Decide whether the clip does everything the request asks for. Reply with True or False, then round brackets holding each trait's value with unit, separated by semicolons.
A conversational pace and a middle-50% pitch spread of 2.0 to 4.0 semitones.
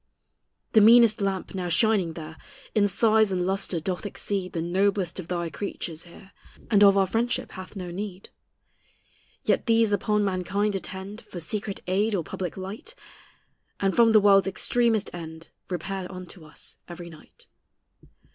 True (155 wpm; 2.8 semitones)